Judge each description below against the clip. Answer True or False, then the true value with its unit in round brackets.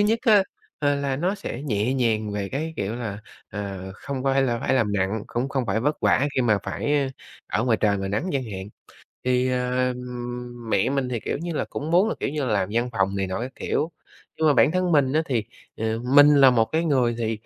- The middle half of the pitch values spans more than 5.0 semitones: False (4.5 semitones)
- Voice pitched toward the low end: True (125 Hz)